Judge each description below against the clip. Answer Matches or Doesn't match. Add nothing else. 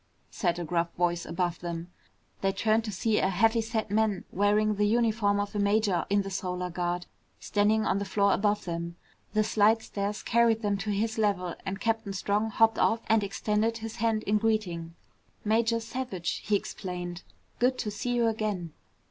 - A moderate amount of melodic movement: Matches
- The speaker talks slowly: Doesn't match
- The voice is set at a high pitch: Matches